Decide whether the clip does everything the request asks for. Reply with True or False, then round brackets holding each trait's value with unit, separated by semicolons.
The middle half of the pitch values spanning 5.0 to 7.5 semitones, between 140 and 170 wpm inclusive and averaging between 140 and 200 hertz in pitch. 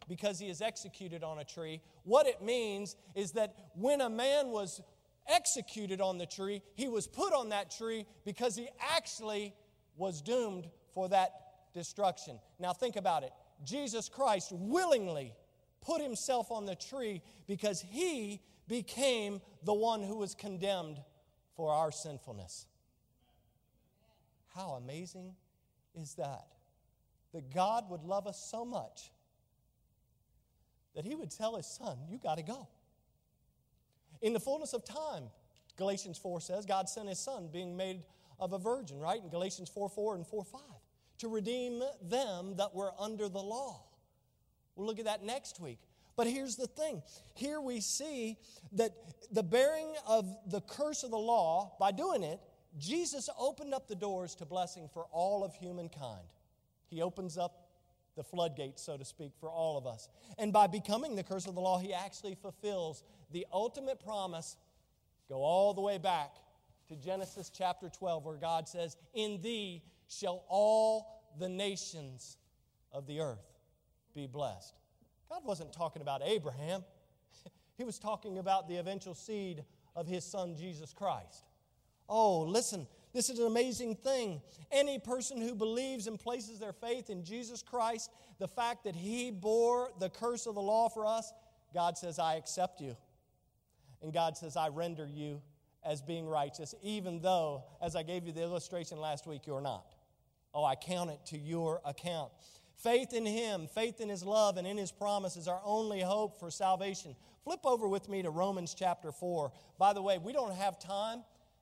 True (5.5 semitones; 165 wpm; 190 Hz)